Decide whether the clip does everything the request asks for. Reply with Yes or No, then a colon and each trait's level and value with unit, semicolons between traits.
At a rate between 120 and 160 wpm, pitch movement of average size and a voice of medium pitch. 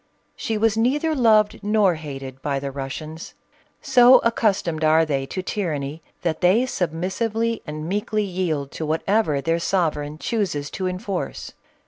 No: average, 140 wpm; wide, 5.8 semitones; medium, 180 Hz